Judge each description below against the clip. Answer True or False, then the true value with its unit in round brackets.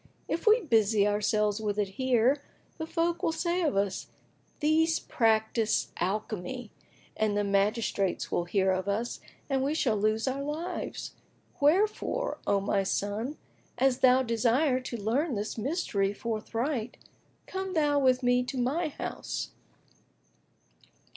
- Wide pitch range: True (5.9 semitones)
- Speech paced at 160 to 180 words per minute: False (135 wpm)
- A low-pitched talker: False (235 Hz)